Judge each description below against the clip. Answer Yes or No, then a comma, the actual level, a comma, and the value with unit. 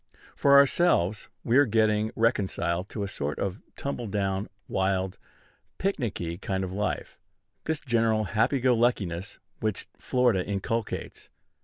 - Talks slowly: Yes, slow, 130 wpm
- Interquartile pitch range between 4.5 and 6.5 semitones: No, average, 4.1 semitones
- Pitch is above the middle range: No, low, 105 Hz